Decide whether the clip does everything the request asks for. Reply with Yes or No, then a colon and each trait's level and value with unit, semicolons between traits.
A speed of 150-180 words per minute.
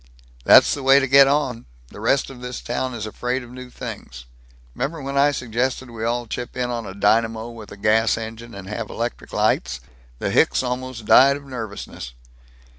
No: average, 190 wpm